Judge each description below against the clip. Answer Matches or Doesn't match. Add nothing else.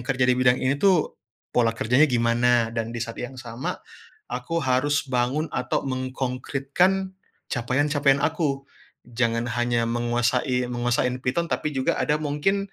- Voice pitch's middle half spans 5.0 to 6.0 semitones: Doesn't match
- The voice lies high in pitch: Doesn't match